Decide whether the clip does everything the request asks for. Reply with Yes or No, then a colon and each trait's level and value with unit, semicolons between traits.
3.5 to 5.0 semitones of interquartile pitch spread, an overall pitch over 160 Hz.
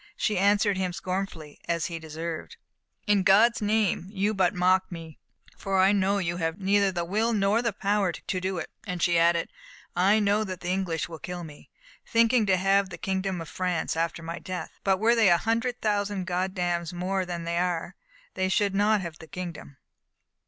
No: average, 2.8 semitones; medium, 185 Hz